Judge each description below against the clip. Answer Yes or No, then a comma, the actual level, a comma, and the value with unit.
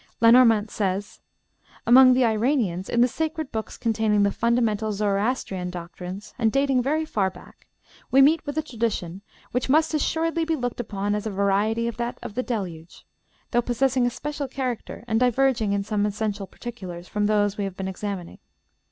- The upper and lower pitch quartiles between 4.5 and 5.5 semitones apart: No, average, 4.0 semitones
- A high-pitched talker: Yes, high, 225 Hz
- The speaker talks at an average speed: Yes, average, 175 wpm